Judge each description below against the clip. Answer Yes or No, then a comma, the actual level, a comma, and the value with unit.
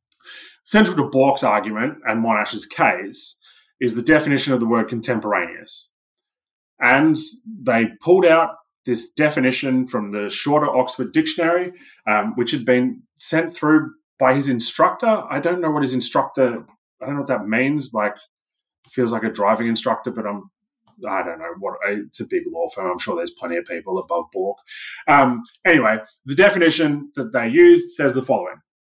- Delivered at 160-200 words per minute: Yes, average, 170 wpm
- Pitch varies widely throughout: Yes, wide, 6.4 semitones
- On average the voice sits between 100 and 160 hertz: Yes, medium, 140 Hz